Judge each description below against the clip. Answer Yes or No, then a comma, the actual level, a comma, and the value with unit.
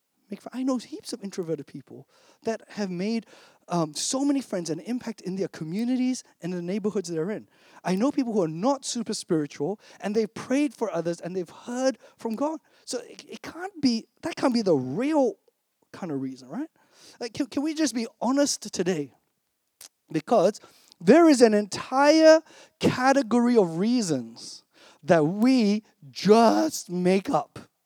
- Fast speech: No, average, 165 wpm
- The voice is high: Yes, high, 225 Hz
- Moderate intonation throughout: No, wide, 6.4 semitones